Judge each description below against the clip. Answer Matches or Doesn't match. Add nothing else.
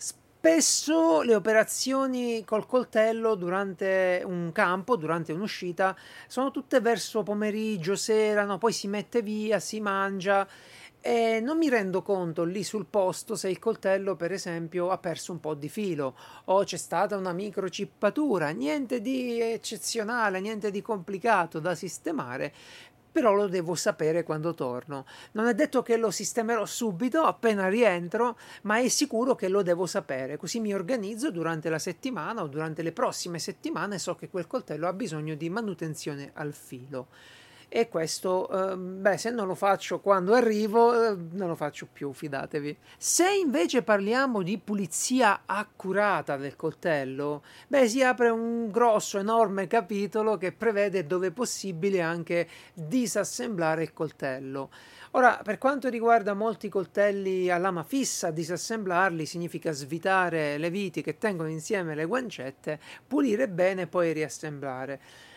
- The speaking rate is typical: Matches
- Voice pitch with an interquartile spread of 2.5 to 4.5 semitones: Doesn't match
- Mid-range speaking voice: Doesn't match